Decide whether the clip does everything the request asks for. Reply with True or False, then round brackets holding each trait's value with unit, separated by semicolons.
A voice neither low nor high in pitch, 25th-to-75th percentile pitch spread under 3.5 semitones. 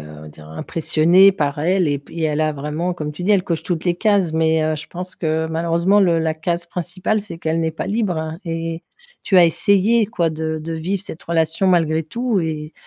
True (165 Hz; 2.6 semitones)